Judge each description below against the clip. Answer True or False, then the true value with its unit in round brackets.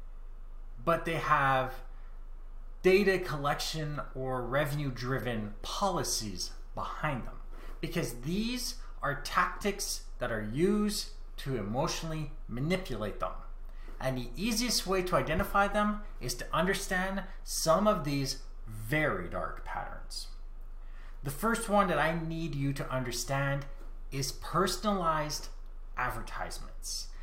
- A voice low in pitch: False (150 Hz)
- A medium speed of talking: False (110 wpm)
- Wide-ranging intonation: True (7.1 semitones)